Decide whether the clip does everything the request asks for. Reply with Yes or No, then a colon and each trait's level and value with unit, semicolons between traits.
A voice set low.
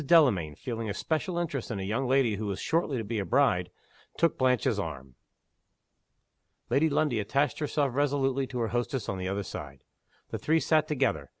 Yes: low, 125 Hz